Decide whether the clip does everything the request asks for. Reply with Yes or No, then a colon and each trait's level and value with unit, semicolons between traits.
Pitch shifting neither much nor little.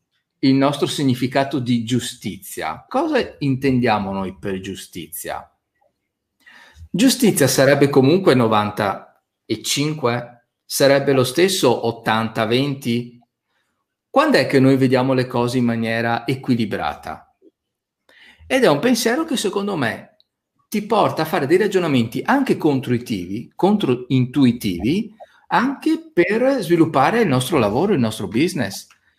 No: wide, 7.1 semitones